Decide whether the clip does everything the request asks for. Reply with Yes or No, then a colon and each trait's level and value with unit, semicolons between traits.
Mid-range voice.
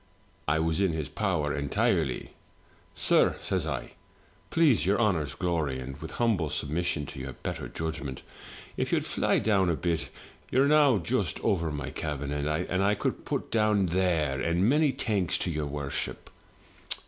No: very low, 85 Hz